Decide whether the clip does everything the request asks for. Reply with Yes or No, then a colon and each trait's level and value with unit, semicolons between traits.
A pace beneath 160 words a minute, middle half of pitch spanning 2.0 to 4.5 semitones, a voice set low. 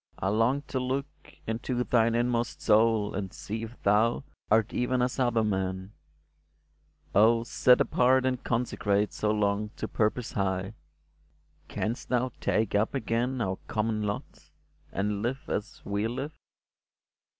Yes: average, 140 wpm; average, 3.0 semitones; low, 115 Hz